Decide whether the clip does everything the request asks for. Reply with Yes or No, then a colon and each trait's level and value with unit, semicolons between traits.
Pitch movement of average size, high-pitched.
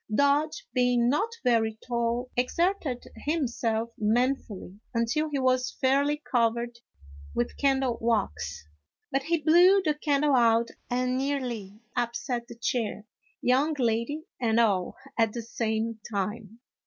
Yes: average, 3.5 semitones; high, 245 Hz